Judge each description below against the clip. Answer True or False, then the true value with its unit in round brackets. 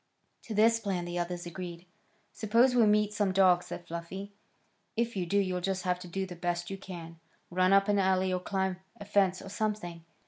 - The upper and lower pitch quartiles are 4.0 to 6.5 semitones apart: False (2.5 semitones)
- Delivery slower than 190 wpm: False (205 wpm)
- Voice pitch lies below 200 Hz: True (190 Hz)